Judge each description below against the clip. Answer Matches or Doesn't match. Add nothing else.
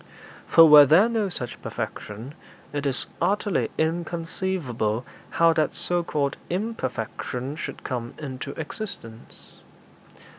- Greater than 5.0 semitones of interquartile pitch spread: Matches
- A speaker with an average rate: Doesn't match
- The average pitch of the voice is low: Doesn't match